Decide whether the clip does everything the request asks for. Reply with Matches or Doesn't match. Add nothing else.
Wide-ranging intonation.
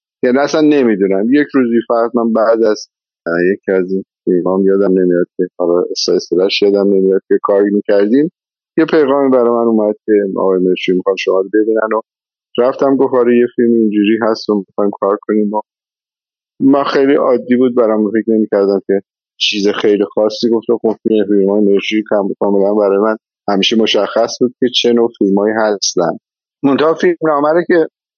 Doesn't match